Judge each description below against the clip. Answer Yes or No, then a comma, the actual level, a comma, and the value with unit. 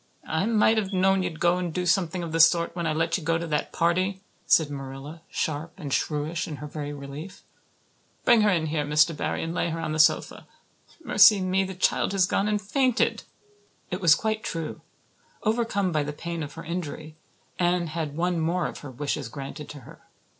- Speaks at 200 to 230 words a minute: Yes, fast, 205 wpm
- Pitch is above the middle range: No, medium, 165 Hz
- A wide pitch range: No, average, 3.4 semitones